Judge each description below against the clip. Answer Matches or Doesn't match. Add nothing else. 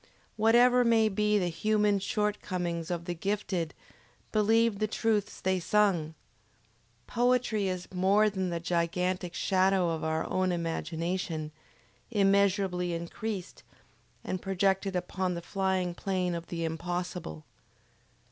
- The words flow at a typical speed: Doesn't match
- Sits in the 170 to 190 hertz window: Matches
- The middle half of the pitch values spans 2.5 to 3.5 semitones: Matches